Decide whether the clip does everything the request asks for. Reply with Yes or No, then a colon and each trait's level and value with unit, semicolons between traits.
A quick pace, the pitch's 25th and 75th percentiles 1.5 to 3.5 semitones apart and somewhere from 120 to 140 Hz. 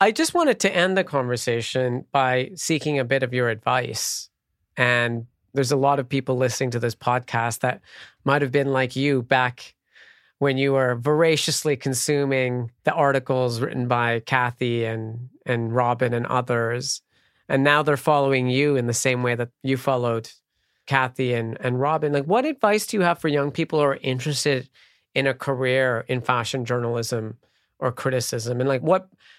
No: average, 175 wpm; narrow, 2.6 semitones; low, 130 Hz